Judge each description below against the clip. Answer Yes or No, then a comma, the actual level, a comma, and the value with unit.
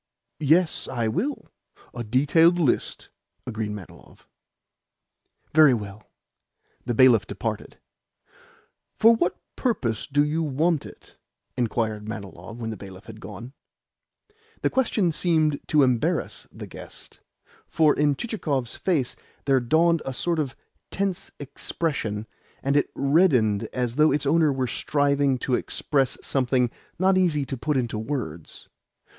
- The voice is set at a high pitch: No, low, 135 Hz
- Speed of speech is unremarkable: No, slow, 130 wpm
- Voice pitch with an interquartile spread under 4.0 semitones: No, average, 5.2 semitones